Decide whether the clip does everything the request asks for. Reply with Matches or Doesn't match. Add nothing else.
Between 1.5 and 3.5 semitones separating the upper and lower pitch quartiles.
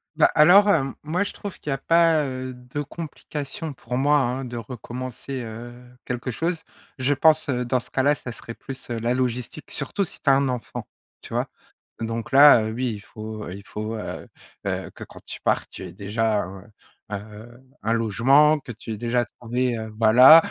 Doesn't match